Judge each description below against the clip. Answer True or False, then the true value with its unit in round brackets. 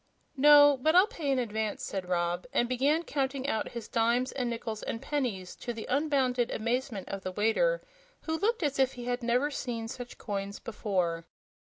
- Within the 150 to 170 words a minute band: False (185 wpm)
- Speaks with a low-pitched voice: False (245 Hz)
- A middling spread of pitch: True (4.4 semitones)